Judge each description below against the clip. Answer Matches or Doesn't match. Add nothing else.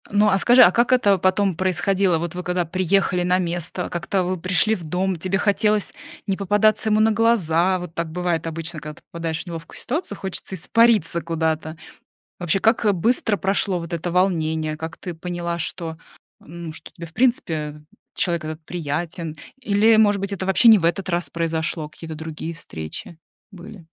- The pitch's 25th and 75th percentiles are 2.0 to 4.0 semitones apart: Matches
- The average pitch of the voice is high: Doesn't match